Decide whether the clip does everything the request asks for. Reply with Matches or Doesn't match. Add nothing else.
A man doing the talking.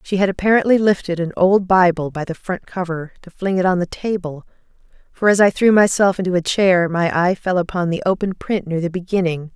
Doesn't match